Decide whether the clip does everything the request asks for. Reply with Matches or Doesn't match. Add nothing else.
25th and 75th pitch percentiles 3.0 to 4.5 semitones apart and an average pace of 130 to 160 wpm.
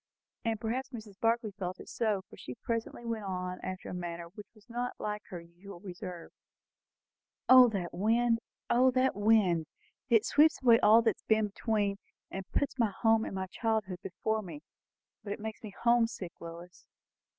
Doesn't match